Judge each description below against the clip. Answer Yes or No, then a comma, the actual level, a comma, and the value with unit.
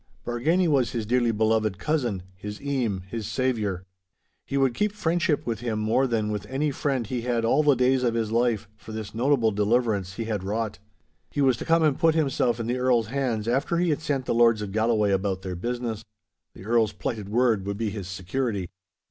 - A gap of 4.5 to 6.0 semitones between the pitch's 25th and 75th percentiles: No, average, 3.8 semitones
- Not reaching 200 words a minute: No, fast, 205 wpm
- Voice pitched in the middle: No, low, 115 Hz